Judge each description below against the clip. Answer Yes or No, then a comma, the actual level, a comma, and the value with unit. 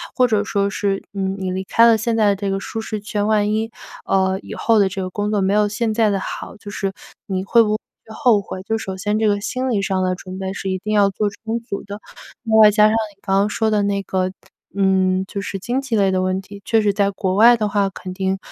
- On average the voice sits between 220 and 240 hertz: No, high, 205 Hz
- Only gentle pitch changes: Yes, narrow, 2.0 semitones